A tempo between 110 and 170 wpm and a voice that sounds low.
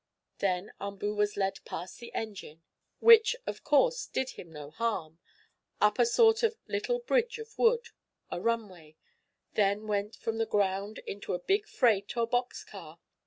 No: average, 165 wpm; high, 215 Hz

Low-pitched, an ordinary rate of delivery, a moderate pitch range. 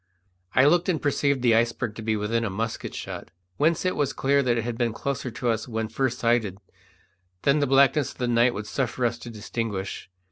No: low, 120 Hz; fast, 215 wpm; average, 3.5 semitones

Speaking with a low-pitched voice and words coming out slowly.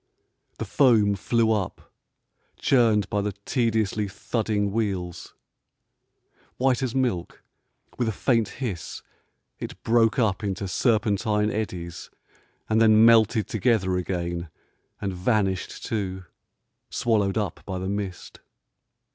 Yes: low, 105 Hz; slow, 115 wpm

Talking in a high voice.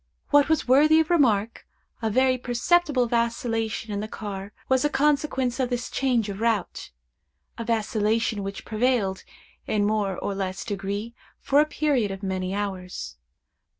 Yes: high, 225 Hz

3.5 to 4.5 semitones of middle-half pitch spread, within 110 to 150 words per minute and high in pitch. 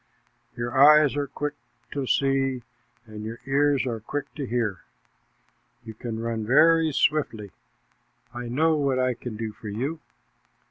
No: average, 4.1 semitones; average, 145 wpm; low, 130 Hz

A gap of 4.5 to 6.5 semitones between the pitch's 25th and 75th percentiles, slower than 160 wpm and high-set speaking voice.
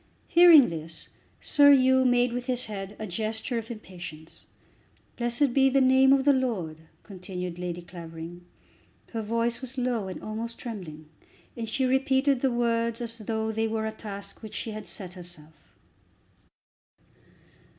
Yes: wide, 5.5 semitones; average, 150 wpm; high, 225 Hz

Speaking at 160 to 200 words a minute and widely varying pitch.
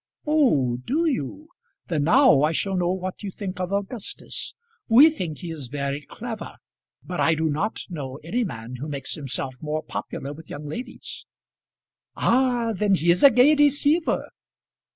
Yes: average, 165 wpm; wide, 8.6 semitones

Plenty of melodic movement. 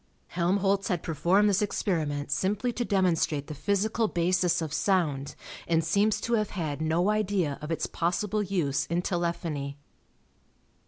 No: average, 4.2 semitones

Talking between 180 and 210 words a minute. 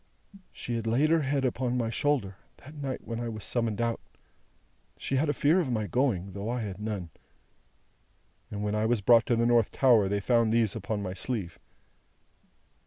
Yes: average, 190 wpm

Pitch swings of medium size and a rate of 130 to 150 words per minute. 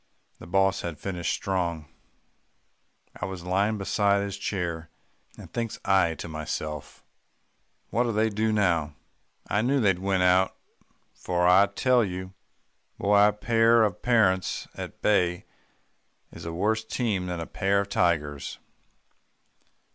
Yes: average, 3.0 semitones; slow, 135 wpm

